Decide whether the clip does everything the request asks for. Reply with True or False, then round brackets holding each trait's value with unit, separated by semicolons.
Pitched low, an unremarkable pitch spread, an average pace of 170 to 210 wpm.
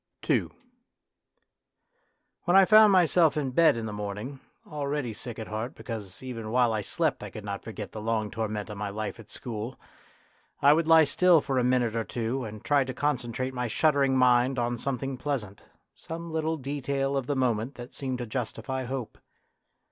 True (125 Hz; 4.1 semitones; 185 wpm)